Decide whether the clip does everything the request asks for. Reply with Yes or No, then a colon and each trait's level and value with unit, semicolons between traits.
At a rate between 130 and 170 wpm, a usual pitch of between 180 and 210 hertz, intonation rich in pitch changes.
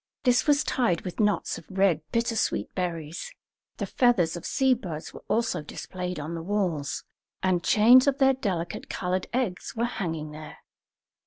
Yes: average, 160 wpm; medium, 185 Hz; wide, 6.1 semitones